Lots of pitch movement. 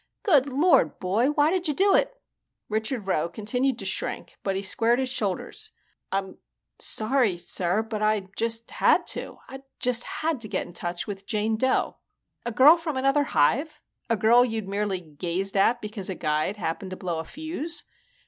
Yes: wide, 5.7 semitones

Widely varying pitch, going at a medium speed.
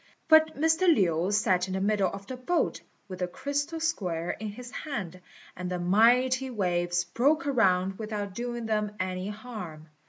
Yes: wide, 5.7 semitones; average, 165 wpm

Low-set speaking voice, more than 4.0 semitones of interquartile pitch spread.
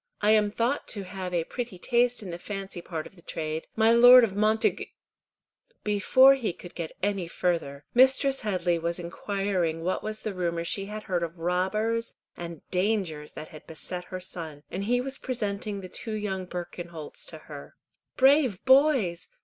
No: high, 195 Hz; average, 4.4 semitones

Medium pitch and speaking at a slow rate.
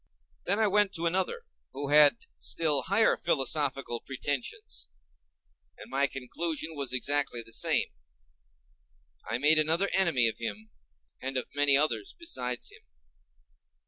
Yes: medium, 145 Hz; slow, 130 wpm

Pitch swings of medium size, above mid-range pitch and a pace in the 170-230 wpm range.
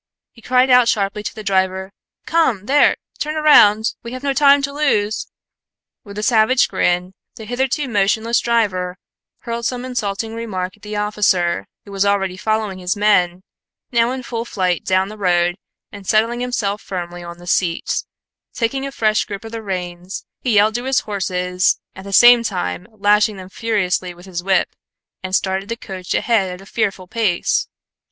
Yes: average, 3.8 semitones; high, 210 Hz; average, 175 wpm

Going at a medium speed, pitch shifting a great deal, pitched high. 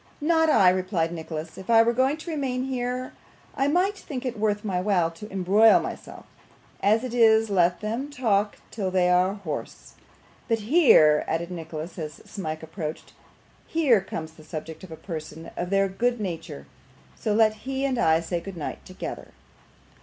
Yes: average, 175 wpm; wide, 6.4 semitones; high, 200 Hz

